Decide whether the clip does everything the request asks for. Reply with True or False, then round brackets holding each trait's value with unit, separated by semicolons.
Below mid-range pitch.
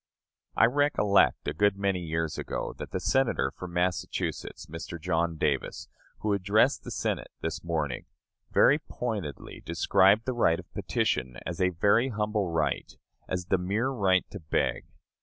True (95 Hz)